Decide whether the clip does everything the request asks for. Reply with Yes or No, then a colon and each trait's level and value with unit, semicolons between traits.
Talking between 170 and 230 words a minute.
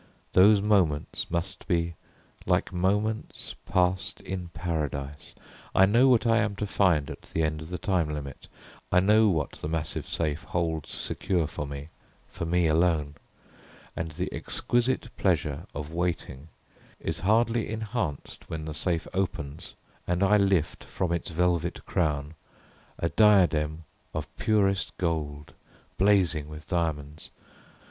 No: average, 140 wpm